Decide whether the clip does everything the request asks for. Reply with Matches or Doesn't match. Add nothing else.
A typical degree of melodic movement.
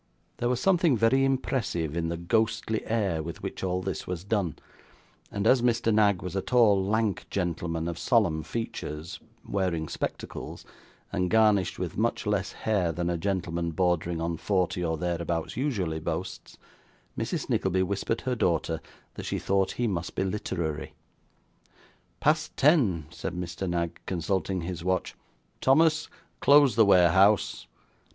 Matches